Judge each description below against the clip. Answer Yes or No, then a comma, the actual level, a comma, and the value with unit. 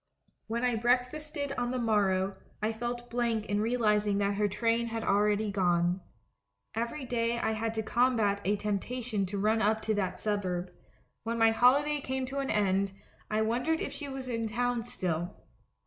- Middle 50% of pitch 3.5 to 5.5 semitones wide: No, average, 3.1 semitones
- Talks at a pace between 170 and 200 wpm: Yes, average, 175 wpm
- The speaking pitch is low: No, high, 225 Hz